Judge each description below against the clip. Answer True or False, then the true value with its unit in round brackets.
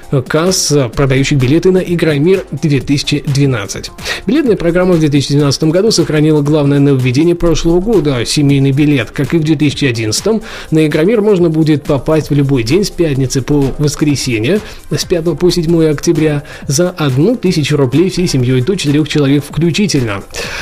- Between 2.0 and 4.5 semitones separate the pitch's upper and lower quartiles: True (3.3 semitones)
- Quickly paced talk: False (140 wpm)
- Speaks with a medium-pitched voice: True (150 Hz)